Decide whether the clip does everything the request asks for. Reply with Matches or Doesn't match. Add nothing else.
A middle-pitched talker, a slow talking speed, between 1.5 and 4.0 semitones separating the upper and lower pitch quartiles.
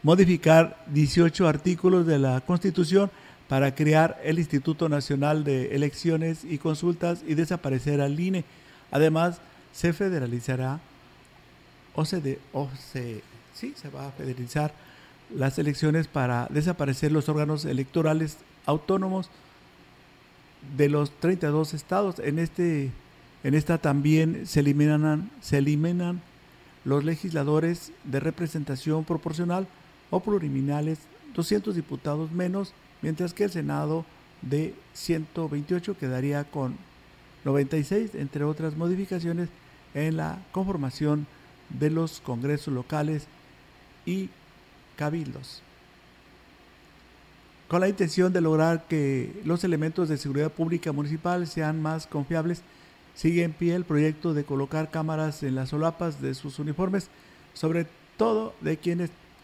Matches